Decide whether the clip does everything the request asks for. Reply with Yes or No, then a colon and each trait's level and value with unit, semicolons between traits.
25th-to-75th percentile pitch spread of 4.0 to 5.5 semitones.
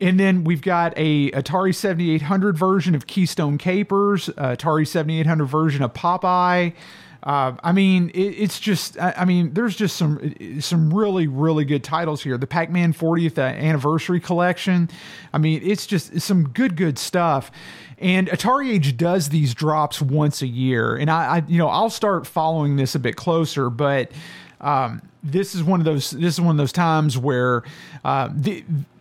No: average, 3.4 semitones